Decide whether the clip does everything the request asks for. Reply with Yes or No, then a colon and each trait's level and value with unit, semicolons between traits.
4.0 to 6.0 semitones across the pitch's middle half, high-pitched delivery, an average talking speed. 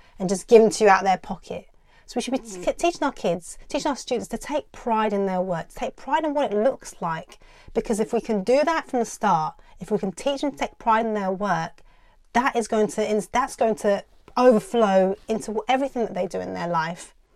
No: average, 4.7 semitones; high, 220 Hz; fast, 250 wpm